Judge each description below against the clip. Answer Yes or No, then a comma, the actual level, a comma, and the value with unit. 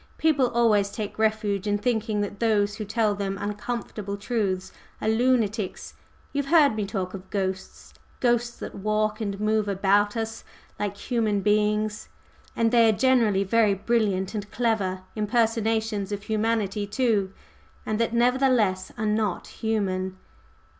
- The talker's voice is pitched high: Yes, high, 215 Hz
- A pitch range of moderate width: No, narrow, 2.2 semitones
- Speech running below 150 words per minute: Yes, average, 140 wpm